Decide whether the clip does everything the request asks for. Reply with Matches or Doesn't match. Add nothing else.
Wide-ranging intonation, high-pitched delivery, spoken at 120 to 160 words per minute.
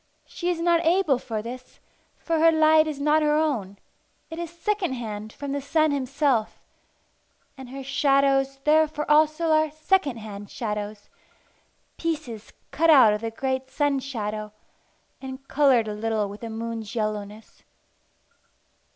Matches